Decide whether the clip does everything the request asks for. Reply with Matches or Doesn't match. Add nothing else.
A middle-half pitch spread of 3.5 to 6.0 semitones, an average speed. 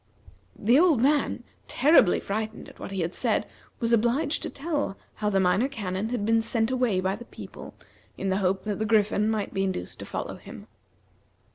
Matches